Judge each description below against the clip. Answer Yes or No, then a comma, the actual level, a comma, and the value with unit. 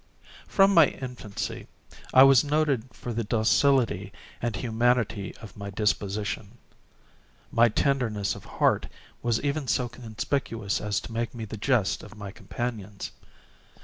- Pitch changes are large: No, average, 3.4 semitones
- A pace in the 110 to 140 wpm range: Yes, slow, 135 wpm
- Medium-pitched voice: No, low, 115 Hz